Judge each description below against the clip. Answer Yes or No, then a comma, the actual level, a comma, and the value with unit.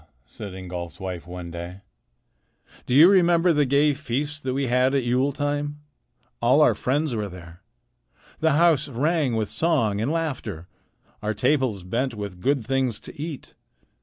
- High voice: No, low, 130 Hz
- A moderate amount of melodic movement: No, wide, 6.3 semitones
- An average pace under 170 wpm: Yes, average, 160 wpm